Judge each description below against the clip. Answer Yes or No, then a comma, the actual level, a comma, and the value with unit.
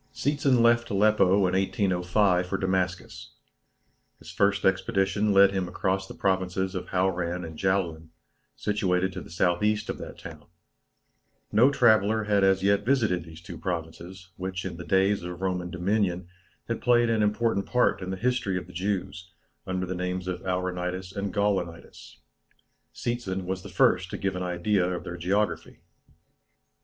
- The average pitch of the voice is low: Yes, very low, 95 Hz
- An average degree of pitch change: No, narrow, 2.2 semitones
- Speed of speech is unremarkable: Yes, average, 160 wpm